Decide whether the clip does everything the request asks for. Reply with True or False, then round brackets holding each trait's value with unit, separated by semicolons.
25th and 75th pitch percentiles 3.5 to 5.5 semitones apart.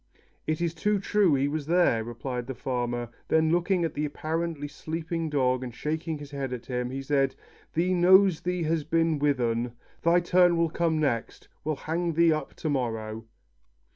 True (4.2 semitones)